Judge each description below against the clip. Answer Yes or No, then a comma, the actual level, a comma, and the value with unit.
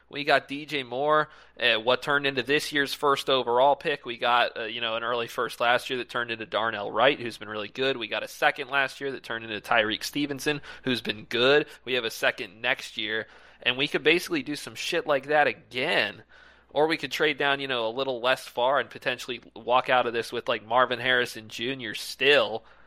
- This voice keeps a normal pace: No, fast, 225 wpm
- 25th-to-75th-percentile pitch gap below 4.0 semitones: Yes, average, 3.1 semitones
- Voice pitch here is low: Yes, low, 130 Hz